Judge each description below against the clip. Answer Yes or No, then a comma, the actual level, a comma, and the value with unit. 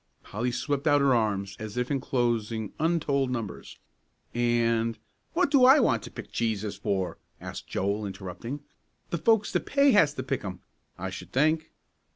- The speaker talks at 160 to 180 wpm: Yes, average, 170 wpm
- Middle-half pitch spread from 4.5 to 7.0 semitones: Yes, wide, 5.4 semitones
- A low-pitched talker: Yes, low, 120 Hz